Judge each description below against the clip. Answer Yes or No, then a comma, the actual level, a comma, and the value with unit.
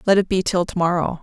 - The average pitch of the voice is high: No, medium, 180 Hz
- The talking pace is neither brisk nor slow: No, fast, 295 wpm